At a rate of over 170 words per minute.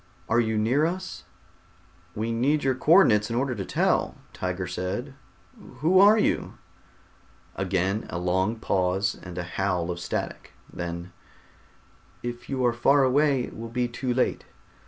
No: average, 155 wpm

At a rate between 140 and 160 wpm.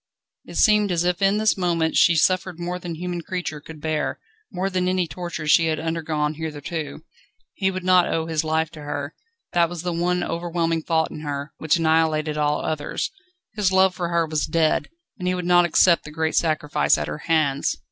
No: average, 200 wpm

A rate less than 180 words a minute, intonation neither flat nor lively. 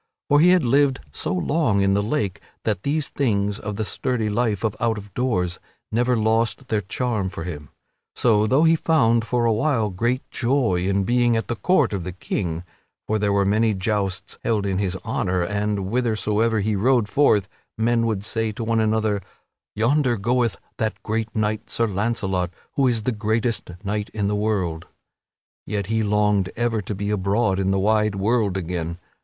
No: average, 185 wpm; average, 3.0 semitones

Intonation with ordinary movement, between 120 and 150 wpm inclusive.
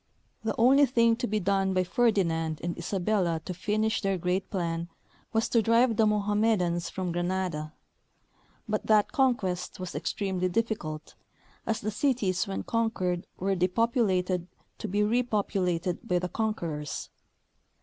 Yes: average, 3.8 semitones; average, 140 wpm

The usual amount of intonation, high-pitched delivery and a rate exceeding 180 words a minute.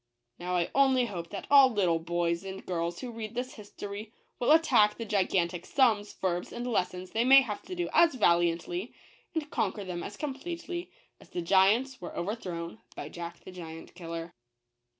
No: wide, 6.2 semitones; high, 200 Hz; average, 190 wpm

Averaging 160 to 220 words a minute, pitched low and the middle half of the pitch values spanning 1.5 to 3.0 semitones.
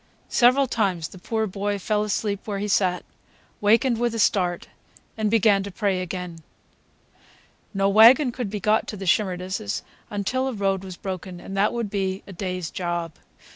No: average, 175 wpm; high, 200 Hz; average, 2.7 semitones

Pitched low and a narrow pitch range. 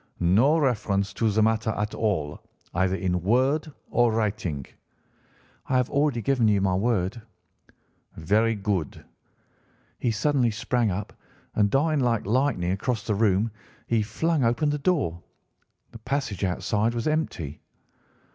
No: low, 110 Hz; average, 4.4 semitones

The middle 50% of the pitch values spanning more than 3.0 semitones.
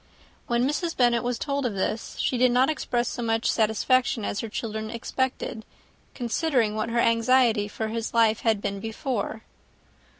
No: narrow, 2.5 semitones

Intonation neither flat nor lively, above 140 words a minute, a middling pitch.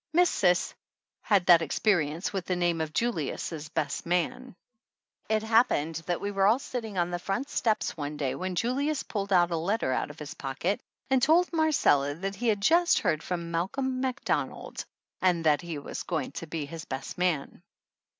No: wide, 6.0 semitones; average, 180 wpm; medium, 180 Hz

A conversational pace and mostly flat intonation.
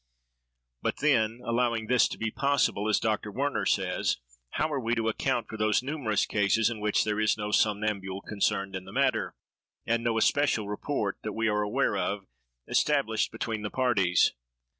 Yes: average, 175 wpm; narrow, 2.3 semitones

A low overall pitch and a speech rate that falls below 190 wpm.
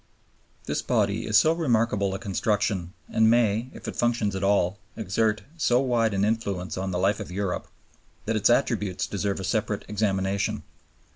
Yes: low, 105 Hz; average, 165 wpm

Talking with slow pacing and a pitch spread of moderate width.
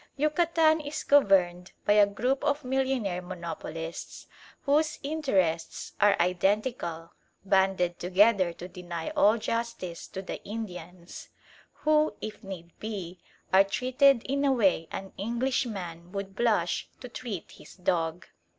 No: slow, 125 wpm; wide, 6.2 semitones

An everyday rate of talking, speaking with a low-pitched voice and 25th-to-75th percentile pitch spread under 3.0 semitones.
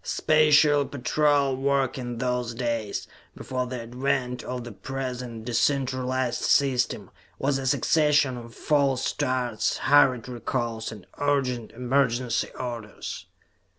No: slow, 120 wpm; low, 125 Hz; narrow, 2.5 semitones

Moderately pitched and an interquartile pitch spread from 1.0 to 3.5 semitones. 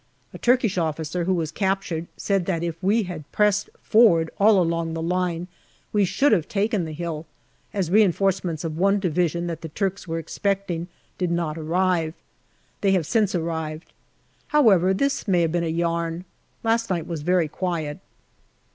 Yes: medium, 175 Hz; average, 3.1 semitones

